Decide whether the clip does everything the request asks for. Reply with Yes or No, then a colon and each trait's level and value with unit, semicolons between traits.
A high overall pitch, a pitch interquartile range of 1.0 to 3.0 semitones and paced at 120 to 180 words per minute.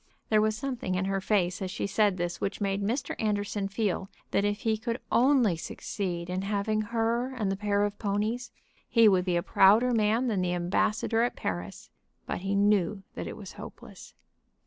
No: high, 205 Hz; average, 2.7 semitones; average, 190 wpm